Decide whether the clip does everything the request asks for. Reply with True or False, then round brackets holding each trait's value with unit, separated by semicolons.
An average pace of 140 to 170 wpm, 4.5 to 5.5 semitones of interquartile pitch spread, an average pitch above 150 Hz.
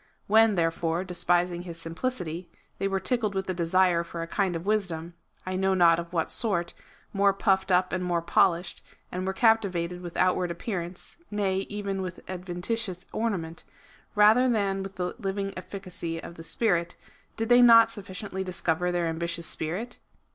False (165 wpm; 2.6 semitones; 185 Hz)